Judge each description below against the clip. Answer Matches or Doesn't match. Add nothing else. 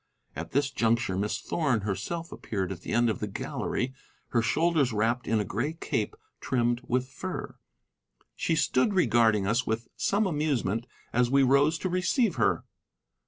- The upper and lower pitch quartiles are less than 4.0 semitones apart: Doesn't match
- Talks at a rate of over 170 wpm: Doesn't match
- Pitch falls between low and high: Doesn't match